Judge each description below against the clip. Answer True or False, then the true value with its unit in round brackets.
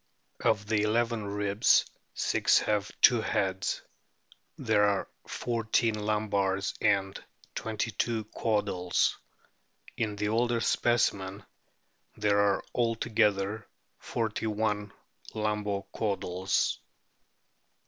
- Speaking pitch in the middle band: False (105 Hz)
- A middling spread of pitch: False (1.7 semitones)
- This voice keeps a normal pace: False (90 wpm)